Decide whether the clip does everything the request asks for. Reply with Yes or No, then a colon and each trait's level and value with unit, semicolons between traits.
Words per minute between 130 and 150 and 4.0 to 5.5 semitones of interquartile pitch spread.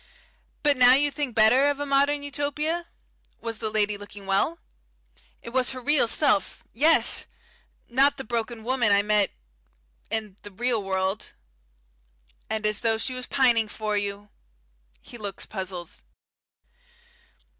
Yes: average, 140 wpm; average, 4.8 semitones